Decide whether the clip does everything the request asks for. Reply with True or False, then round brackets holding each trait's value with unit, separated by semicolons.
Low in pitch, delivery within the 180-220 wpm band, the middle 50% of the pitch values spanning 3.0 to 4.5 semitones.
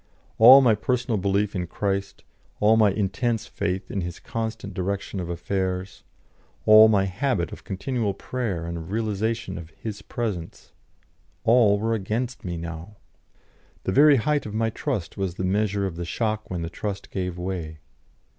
False (100 Hz; 165 wpm; 3.4 semitones)